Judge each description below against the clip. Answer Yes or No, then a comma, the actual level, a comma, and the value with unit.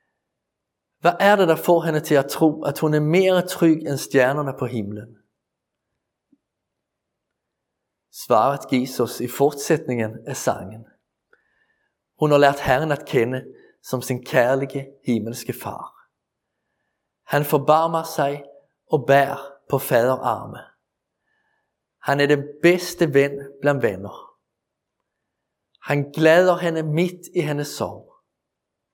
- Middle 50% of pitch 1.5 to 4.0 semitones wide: Yes, average, 3.4 semitones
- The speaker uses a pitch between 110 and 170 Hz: Yes, medium, 140 Hz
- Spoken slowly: Yes, slow, 120 wpm